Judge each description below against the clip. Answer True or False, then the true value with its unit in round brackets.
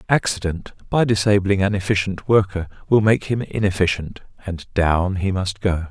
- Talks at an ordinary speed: True (150 wpm)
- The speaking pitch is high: False (95 Hz)